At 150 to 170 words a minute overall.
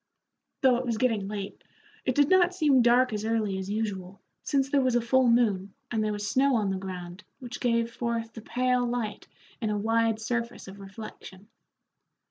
No: average, 190 wpm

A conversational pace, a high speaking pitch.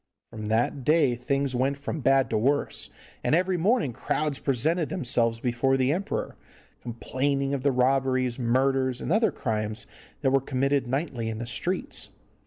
No: average, 160 wpm; low, 135 Hz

